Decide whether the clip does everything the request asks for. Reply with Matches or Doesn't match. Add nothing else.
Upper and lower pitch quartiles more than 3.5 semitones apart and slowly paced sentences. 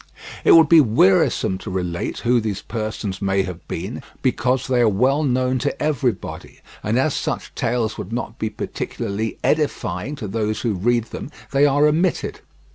Doesn't match